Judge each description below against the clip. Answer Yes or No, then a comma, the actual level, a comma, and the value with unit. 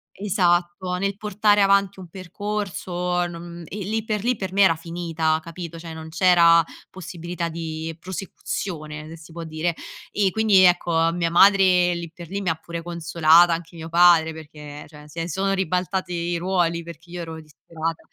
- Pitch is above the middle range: No, medium, 175 Hz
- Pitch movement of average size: No, narrow, 2.3 semitones